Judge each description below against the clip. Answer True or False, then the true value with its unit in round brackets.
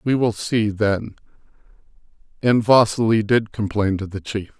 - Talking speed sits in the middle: True (145 wpm)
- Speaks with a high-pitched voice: False (105 Hz)